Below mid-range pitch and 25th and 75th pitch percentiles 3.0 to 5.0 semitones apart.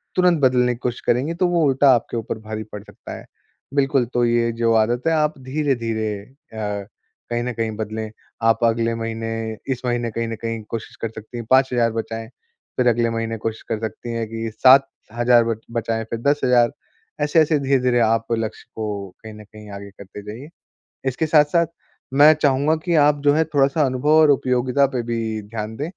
Yes: low, 120 Hz; average, 3.3 semitones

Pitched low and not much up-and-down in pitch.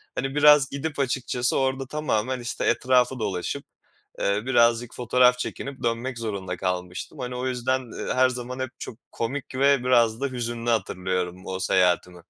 No: low, 125 Hz; average, 3.4 semitones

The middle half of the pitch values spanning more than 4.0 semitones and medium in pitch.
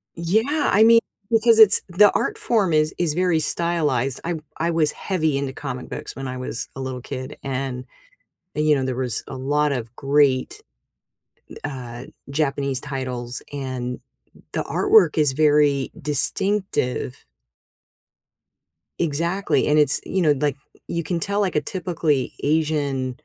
Yes: average, 4.4 semitones; medium, 150 Hz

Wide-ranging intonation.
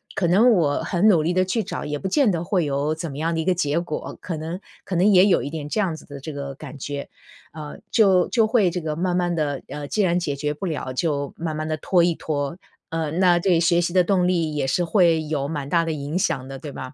No: average, 3.5 semitones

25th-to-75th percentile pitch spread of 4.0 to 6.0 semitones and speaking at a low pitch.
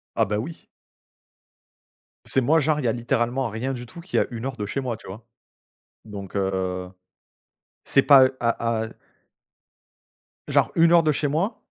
Yes: average, 4.6 semitones; low, 120 Hz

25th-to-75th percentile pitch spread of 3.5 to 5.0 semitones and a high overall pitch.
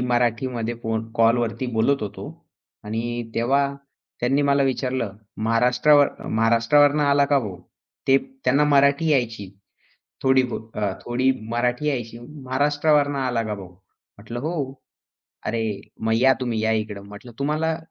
No: average, 3.8 semitones; low, 125 Hz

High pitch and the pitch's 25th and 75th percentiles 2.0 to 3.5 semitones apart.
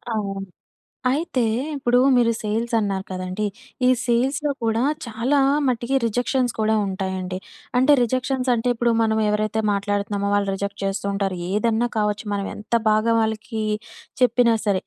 Yes: high, 220 Hz; average, 3.2 semitones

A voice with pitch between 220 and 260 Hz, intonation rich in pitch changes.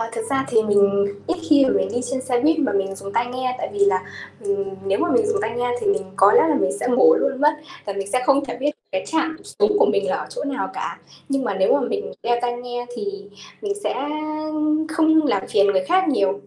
Yes: very high, 255 Hz; wide, 7.5 semitones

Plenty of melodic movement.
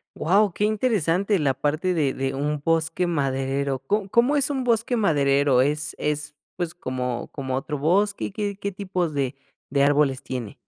Yes: wide, 6.4 semitones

